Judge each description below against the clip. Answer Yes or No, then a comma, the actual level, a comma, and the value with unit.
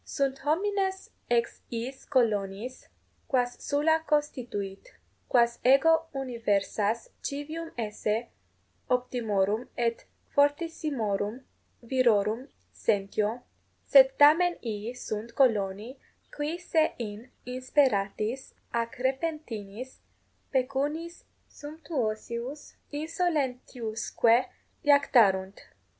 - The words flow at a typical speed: No, slow, 75 wpm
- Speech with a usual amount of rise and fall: Yes, average, 4.9 semitones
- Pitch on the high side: Yes, very high, 250 Hz